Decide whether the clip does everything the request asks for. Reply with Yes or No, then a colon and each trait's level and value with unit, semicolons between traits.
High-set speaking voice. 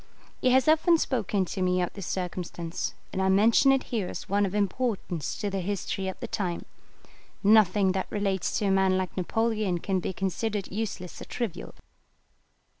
Yes: high, 195 Hz